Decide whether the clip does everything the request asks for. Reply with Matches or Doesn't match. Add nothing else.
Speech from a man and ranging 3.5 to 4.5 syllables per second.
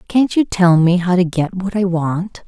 Doesn't match